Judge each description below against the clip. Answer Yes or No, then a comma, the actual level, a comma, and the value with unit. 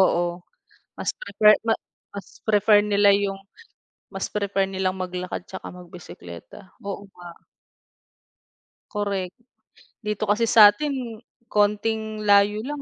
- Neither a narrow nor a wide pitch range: No, narrow, 2.0 semitones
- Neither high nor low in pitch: No, high, 200 Hz